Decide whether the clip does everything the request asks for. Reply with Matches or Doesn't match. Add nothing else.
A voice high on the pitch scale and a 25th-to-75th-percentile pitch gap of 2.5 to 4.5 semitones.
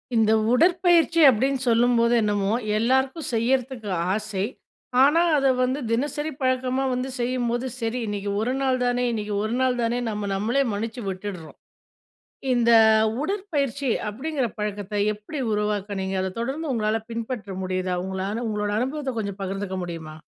Matches